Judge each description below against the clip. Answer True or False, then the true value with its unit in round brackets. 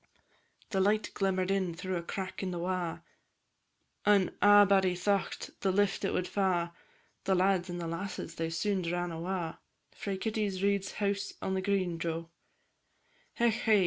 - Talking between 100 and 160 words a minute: True (155 wpm)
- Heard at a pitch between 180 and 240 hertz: True (190 Hz)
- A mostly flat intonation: True (2.2 semitones)